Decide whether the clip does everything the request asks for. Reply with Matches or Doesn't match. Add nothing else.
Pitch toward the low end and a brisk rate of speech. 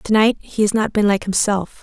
Doesn't match